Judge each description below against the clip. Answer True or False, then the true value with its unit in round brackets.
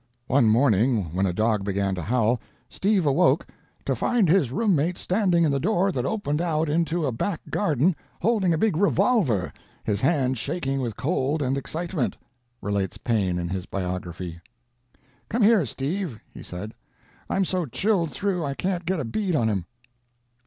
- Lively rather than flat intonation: True (8.7 semitones)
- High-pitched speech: False (140 Hz)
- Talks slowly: False (170 wpm)